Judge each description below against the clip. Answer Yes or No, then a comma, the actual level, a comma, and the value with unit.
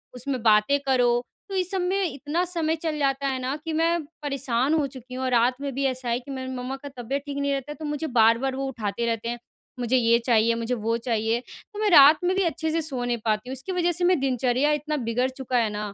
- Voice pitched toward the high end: Yes, very high, 265 Hz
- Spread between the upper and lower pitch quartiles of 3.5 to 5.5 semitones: Yes, average, 3.9 semitones